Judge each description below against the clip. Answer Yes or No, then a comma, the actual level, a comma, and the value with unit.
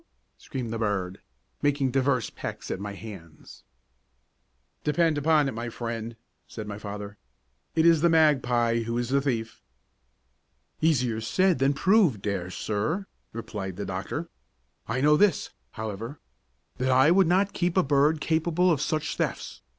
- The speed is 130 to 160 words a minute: Yes, average, 150 wpm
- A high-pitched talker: No, low, 130 Hz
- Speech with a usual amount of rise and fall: No, wide, 6.1 semitones